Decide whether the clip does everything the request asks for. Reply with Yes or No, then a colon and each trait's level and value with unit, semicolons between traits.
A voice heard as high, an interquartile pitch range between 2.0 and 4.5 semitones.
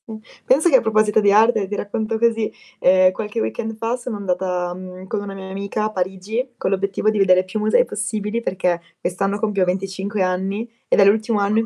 Yes: high, 205 Hz; narrow, 2.6 semitones